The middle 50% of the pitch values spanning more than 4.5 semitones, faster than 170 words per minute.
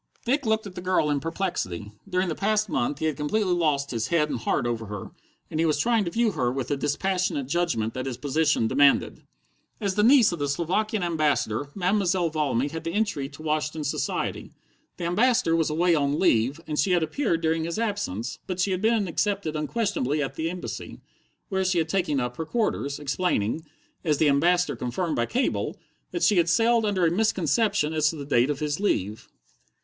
Yes: average, 5.1 semitones; fast, 205 wpm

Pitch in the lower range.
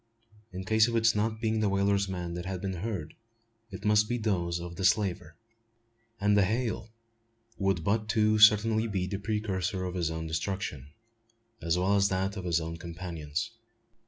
Yes: very low, 95 Hz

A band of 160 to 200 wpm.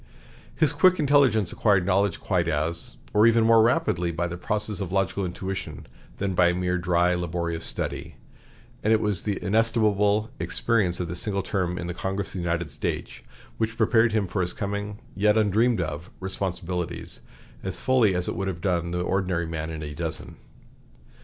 Yes: average, 175 wpm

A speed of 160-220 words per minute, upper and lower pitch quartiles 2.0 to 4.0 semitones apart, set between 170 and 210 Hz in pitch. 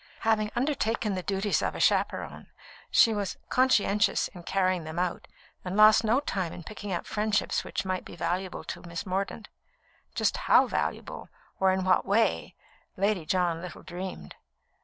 Yes: average, 165 wpm; average, 2.9 semitones; high, 190 Hz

